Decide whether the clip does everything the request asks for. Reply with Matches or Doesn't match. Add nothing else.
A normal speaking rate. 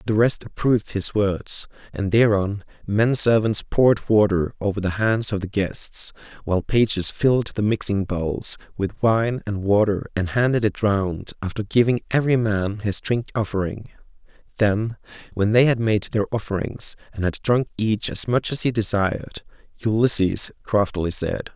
Matches